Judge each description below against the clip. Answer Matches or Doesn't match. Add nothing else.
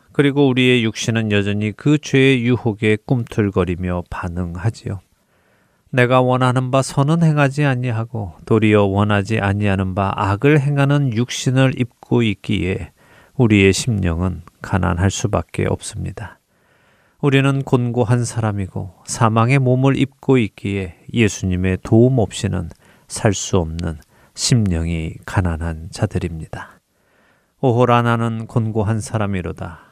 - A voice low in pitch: Matches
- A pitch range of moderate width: Matches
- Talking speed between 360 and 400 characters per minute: Doesn't match